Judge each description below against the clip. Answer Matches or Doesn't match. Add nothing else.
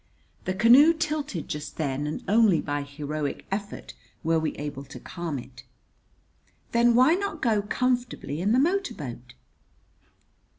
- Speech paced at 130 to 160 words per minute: Matches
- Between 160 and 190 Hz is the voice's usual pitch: Matches